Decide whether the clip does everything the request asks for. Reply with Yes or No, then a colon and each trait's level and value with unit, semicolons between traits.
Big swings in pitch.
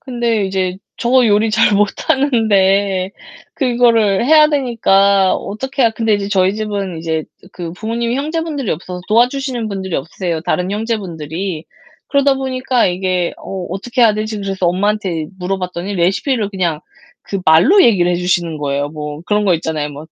No: average, 4.7 semitones